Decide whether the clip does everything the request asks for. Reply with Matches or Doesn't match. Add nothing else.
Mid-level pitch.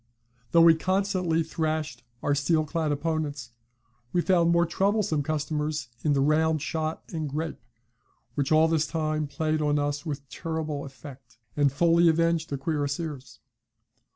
Matches